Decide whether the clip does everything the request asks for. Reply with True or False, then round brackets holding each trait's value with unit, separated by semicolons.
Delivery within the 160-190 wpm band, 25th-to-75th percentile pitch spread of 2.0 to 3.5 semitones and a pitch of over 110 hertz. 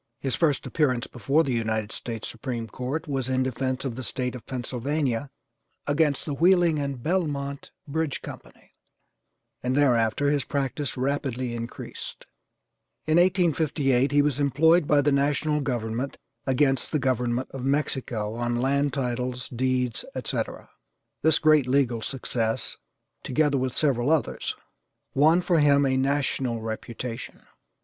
False (140 wpm; 2.9 semitones; 135 Hz)